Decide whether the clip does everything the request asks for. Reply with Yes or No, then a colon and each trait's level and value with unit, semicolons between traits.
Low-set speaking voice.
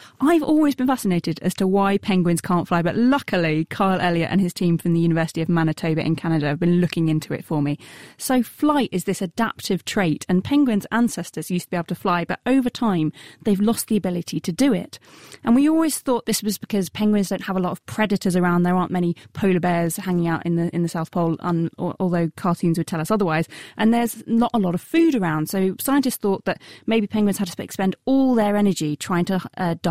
No: medium, 185 Hz